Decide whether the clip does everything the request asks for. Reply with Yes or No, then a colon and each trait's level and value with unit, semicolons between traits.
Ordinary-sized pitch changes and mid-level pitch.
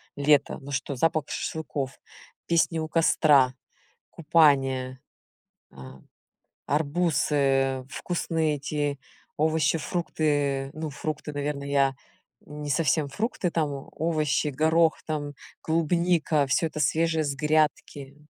No: narrow, 2.3 semitones; medium, 150 Hz